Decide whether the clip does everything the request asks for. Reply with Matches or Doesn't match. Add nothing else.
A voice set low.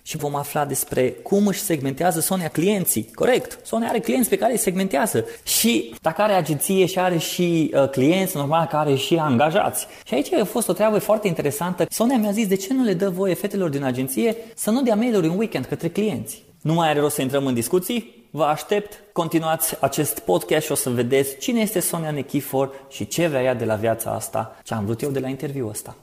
Doesn't match